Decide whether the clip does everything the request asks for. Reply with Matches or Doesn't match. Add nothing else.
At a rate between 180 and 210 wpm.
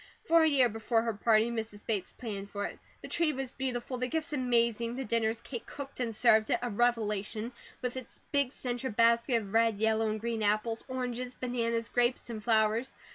Matches